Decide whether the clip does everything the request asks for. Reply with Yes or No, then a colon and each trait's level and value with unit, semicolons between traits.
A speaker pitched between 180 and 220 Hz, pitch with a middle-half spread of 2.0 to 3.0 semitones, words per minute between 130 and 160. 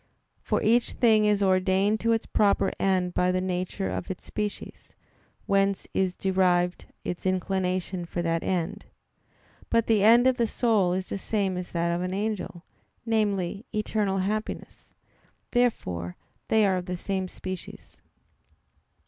Yes: high, 190 Hz; average, 2.7 semitones; average, 150 wpm